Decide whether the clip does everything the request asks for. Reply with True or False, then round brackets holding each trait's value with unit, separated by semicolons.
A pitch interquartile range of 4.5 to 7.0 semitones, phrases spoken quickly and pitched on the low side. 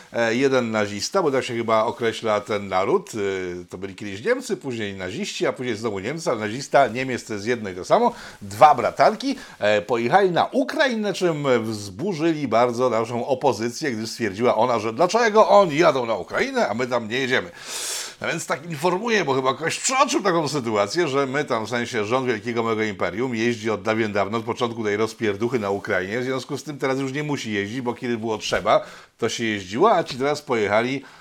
True (5.1 semitones; 190 wpm; 120 Hz)